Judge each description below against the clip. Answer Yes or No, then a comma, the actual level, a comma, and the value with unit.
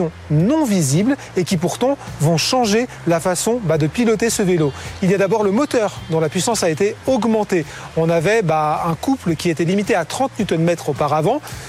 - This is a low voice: No, medium, 185 Hz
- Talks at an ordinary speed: Yes, average, 185 wpm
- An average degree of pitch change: No, wide, 5.7 semitones